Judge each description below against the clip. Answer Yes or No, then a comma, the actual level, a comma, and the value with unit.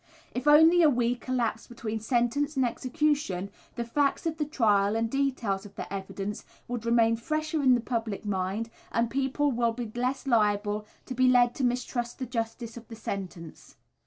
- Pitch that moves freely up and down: No, average, 3.3 semitones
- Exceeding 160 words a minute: Yes, average, 180 wpm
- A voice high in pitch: Yes, high, 235 Hz